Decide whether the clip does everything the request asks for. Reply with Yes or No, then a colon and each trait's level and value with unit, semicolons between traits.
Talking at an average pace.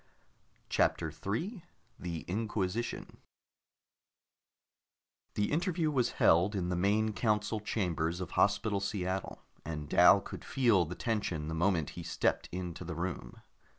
No: slow, 125 wpm